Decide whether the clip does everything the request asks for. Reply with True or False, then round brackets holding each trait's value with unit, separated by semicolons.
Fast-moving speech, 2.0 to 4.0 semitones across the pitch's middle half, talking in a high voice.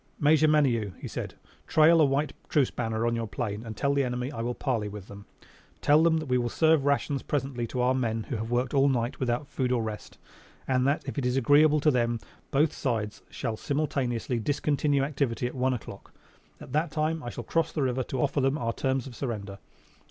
False (220 wpm; 3.6 semitones; 130 Hz)